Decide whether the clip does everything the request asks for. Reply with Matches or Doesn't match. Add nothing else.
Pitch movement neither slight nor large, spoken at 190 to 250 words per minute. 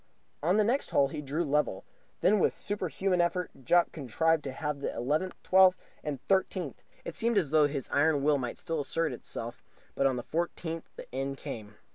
Matches